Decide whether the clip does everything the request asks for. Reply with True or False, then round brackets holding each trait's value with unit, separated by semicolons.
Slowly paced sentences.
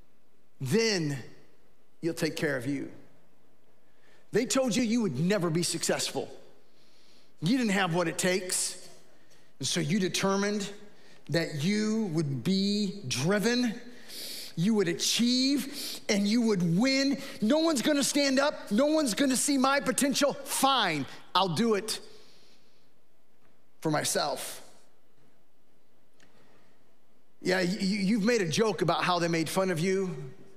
True (130 wpm)